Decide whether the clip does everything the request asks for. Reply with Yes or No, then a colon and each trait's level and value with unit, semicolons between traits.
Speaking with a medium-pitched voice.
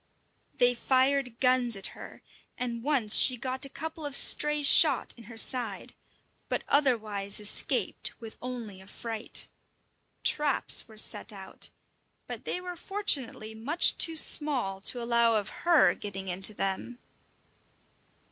No: high, 240 Hz